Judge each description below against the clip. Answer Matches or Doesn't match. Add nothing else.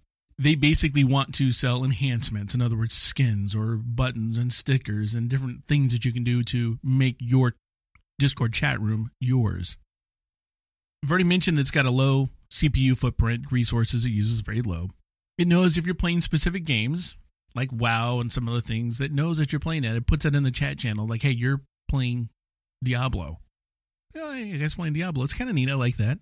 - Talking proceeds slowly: Doesn't match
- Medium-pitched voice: Doesn't match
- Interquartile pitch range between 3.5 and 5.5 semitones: Matches